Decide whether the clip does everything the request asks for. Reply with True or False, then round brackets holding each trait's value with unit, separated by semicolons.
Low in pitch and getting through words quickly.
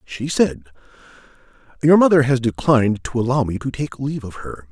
False (130 Hz; 180 wpm)